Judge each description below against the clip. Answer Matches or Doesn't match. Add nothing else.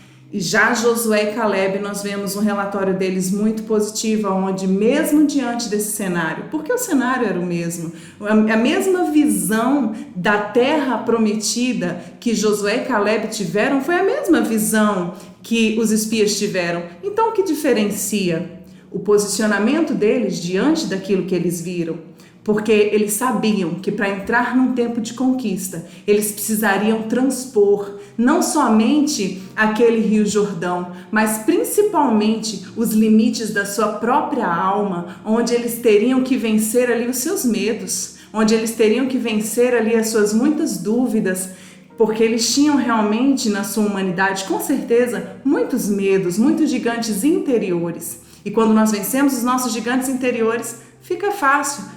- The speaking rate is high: Doesn't match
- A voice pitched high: Matches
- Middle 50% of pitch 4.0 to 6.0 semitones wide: Doesn't match